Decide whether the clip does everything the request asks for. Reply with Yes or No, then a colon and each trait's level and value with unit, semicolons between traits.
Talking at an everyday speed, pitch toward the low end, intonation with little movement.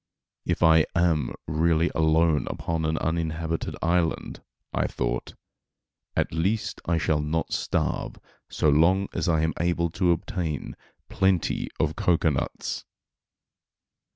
No: slow, 120 wpm; very low, 80 Hz; narrow, 1.4 semitones